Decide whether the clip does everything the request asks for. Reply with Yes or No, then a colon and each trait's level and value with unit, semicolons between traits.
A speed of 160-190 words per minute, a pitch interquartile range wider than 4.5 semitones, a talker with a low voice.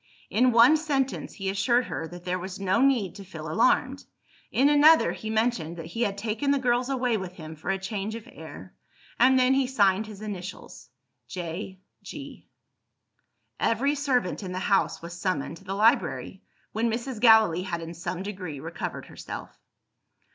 No: average, 175 wpm; average, 5.2 semitones; high, 210 Hz